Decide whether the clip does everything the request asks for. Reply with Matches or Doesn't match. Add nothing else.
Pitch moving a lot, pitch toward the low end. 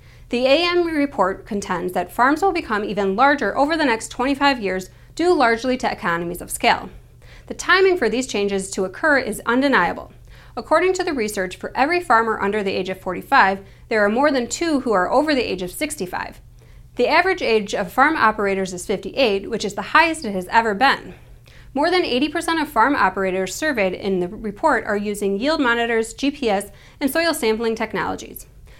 Doesn't match